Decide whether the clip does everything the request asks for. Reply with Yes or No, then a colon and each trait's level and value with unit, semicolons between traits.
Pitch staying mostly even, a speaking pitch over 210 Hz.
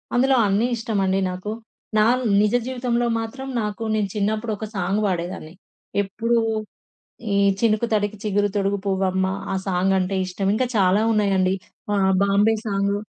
No: narrow, 2.2 semitones; high, 205 Hz